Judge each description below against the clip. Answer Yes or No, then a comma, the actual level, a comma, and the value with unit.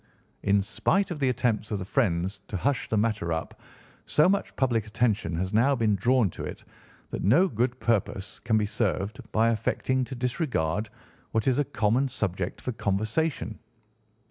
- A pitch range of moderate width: Yes, average, 4.2 semitones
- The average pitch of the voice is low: Yes, low, 110 Hz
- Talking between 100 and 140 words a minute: No, average, 170 wpm